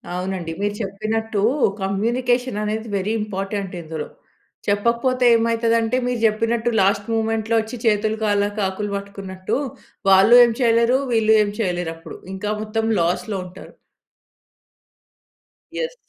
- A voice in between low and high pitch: No, high, 215 Hz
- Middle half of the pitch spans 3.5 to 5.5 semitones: No, average, 2.7 semitones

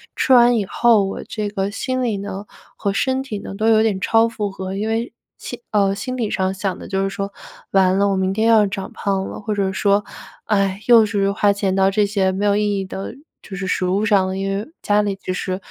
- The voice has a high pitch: Yes, high, 200 Hz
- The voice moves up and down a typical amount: No, narrow, 2.0 semitones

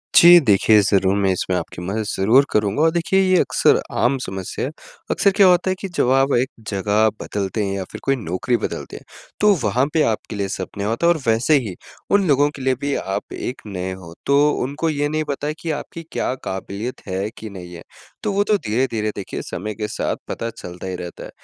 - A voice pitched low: Yes, low, 115 Hz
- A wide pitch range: Yes, wide, 7.0 semitones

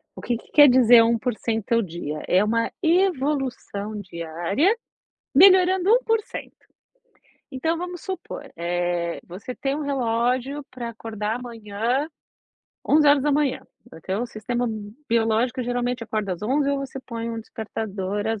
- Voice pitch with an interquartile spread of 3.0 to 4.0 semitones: No, average, 4.8 semitones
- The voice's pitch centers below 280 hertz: Yes, high, 235 Hz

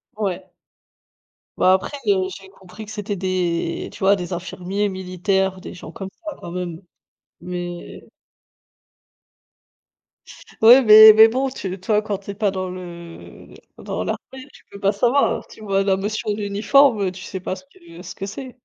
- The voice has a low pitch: No, high, 195 Hz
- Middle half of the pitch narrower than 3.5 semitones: Yes, average, 2.8 semitones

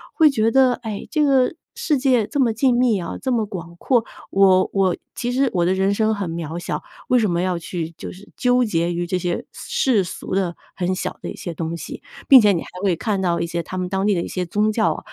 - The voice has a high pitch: Yes, high, 195 Hz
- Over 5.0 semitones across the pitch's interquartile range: Yes, wide, 5.6 semitones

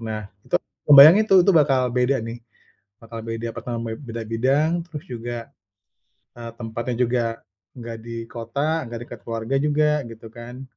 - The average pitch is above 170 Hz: No, low, 120 Hz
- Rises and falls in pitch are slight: No, average, 3.3 semitones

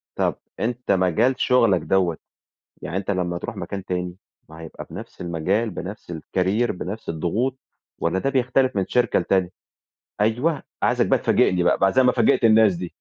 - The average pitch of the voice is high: No, very low, 95 Hz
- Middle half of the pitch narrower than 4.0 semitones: No, average, 5.2 semitones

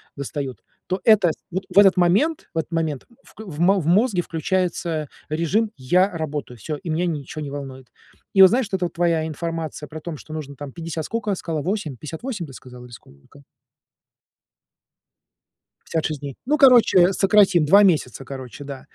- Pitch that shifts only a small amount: No, average, 4.7 semitones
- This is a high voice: No, medium, 165 Hz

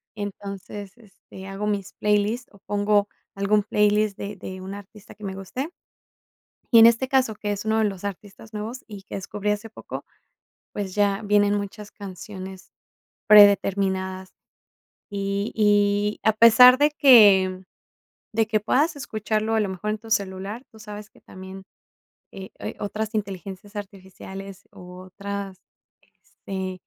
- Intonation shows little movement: Yes, narrow, 1.7 semitones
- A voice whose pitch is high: Yes, high, 205 Hz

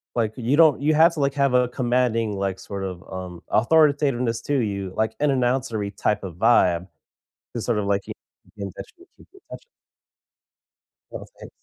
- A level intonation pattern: No, wide, 5.6 semitones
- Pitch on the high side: No, low, 115 Hz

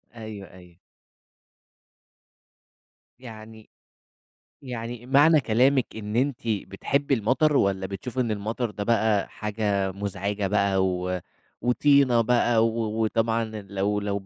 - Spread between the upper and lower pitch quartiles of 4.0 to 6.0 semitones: No, average, 3.4 semitones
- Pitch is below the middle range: Yes, low, 110 Hz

